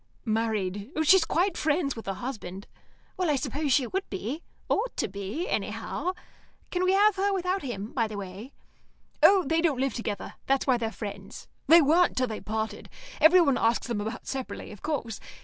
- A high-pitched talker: Yes, very high, 260 Hz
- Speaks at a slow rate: No, average, 185 wpm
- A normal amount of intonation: No, wide, 7.2 semitones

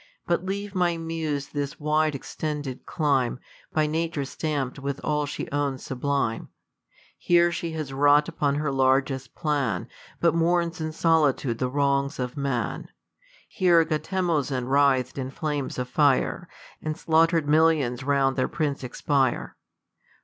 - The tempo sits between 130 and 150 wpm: Yes, average, 140 wpm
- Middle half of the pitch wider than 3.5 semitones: No, average, 3.1 semitones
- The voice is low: No, medium, 145 Hz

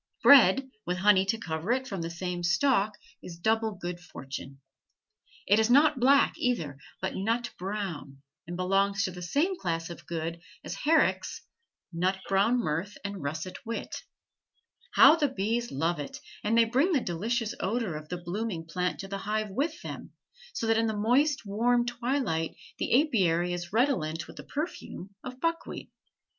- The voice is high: Yes, high, 200 Hz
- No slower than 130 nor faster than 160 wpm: No, average, 170 wpm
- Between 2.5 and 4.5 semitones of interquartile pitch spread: No, wide, 5.6 semitones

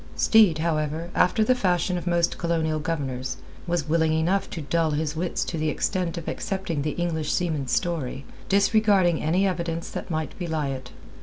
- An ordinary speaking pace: Yes, average, 170 wpm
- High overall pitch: No, medium, 165 Hz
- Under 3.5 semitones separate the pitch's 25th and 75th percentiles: Yes, narrow, 2.4 semitones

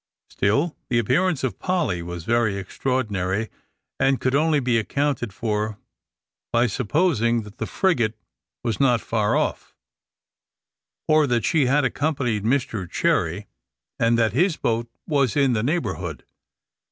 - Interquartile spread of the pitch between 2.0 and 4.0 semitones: No, average, 4.8 semitones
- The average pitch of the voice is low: Yes, low, 120 Hz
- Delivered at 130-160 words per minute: Yes, slow, 135 wpm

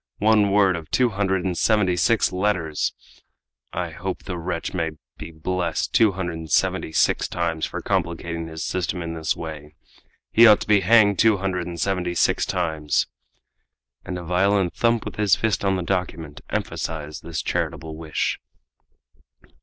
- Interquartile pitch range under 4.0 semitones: Yes, average, 3.4 semitones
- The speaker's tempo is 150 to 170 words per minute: Yes, average, 165 wpm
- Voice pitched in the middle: No, very low, 90 Hz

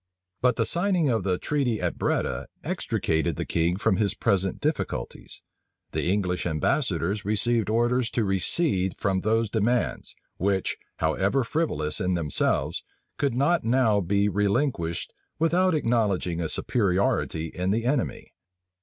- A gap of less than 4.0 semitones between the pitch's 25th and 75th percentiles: No, average, 5.1 semitones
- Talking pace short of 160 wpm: Yes, slow, 135 wpm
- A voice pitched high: No, low, 105 Hz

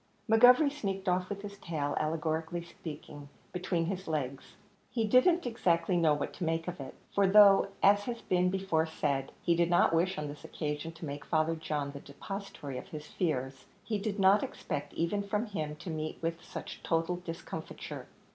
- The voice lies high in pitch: No, medium, 170 Hz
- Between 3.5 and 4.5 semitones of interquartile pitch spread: Yes, average, 4.2 semitones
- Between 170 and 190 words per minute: Yes, average, 185 wpm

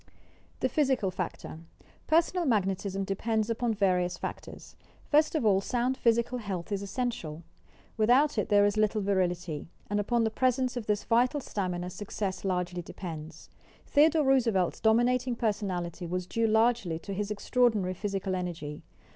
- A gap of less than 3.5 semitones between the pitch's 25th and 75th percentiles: No, average, 4.7 semitones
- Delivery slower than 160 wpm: Yes, average, 145 wpm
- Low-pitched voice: No, high, 205 Hz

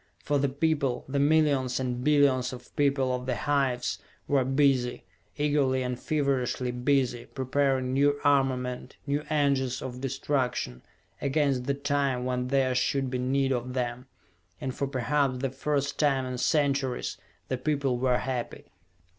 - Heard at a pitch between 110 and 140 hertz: Yes, low, 135 Hz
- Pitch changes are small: Yes, narrow, 2.0 semitones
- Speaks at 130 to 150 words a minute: Yes, average, 145 wpm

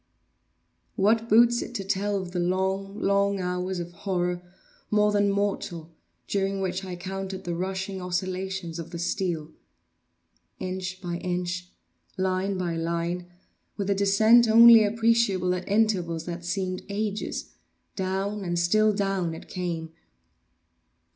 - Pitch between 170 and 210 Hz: Yes, high, 190 Hz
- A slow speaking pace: Yes, slow, 125 wpm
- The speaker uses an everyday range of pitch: No, narrow, 2.2 semitones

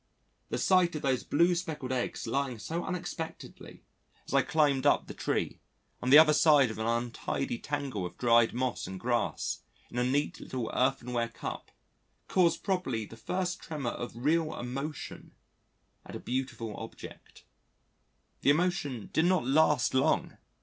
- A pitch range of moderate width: Yes, average, 4.7 semitones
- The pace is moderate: Yes, average, 155 wpm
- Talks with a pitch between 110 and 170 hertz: Yes, low, 135 Hz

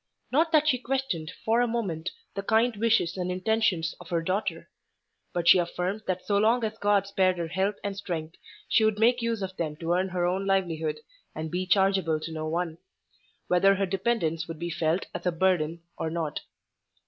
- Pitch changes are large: No, average, 4.0 semitones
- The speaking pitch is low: No, medium, 185 Hz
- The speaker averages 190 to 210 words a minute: Yes, average, 195 wpm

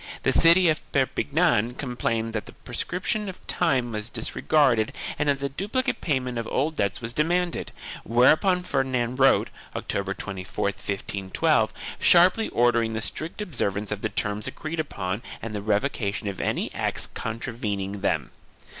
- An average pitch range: No, wide, 6.6 semitones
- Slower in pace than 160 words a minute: Yes, average, 145 wpm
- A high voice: No, low, 120 Hz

